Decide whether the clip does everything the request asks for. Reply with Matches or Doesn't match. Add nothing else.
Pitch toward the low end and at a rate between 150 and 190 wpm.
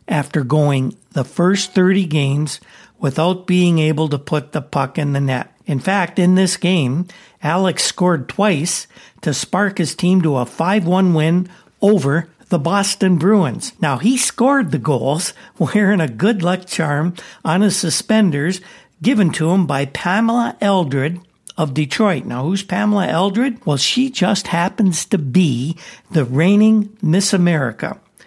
Doesn't match